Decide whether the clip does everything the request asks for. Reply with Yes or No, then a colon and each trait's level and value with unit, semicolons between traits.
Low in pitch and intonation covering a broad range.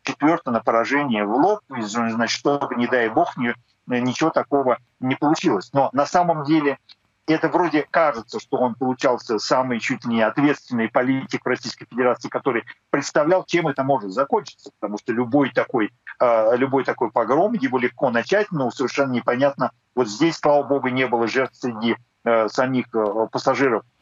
No: low, 130 Hz; average, 3.5 semitones